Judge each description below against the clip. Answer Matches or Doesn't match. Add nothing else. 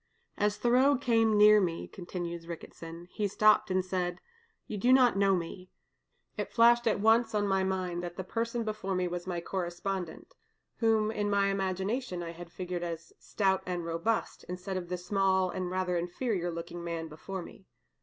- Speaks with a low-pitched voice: Doesn't match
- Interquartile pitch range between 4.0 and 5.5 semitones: Doesn't match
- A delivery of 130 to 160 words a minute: Doesn't match